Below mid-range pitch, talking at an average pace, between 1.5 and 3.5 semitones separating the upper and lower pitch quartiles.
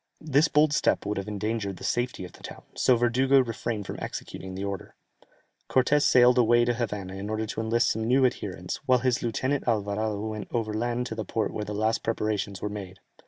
No: low, 110 Hz; fast, 210 wpm; average, 3.0 semitones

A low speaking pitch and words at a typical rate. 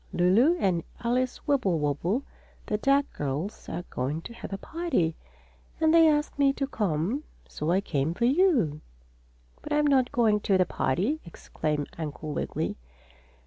No: high, 210 Hz; average, 150 wpm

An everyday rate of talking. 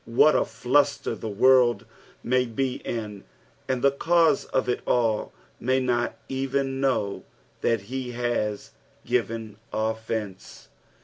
No: slow, 120 wpm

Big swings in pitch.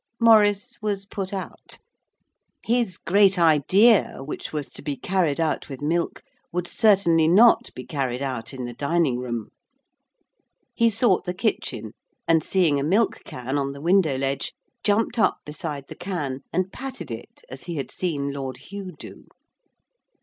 Yes: wide, 6.1 semitones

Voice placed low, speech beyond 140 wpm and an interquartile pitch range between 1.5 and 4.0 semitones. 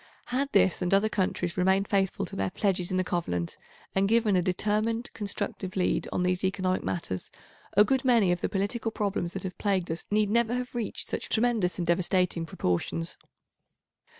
No: high, 190 Hz; average, 180 wpm; average, 3.1 semitones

